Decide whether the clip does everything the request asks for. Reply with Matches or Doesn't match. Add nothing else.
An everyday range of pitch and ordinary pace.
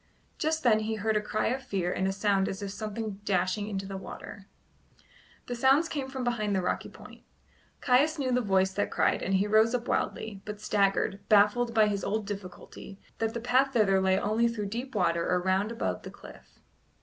Doesn't match